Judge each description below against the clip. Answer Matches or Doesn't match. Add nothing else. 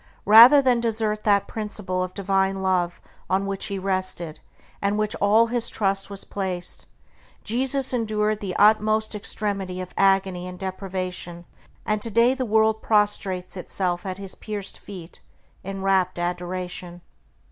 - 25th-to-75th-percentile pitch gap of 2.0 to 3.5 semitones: Matches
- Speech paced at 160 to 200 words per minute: Doesn't match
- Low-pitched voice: Doesn't match